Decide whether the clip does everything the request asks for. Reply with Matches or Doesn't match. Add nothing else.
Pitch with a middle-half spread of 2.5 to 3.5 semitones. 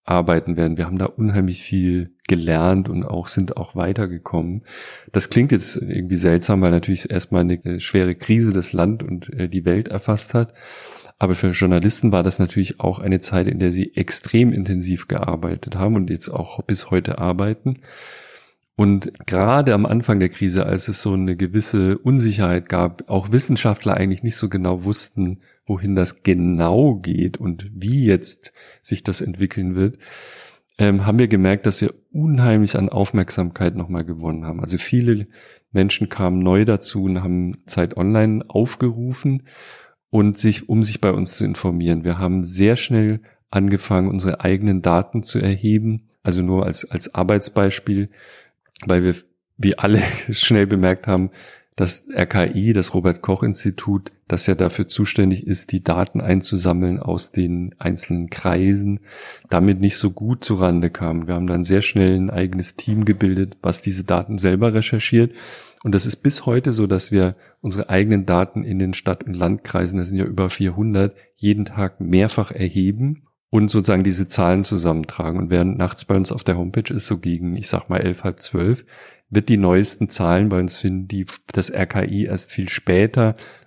Matches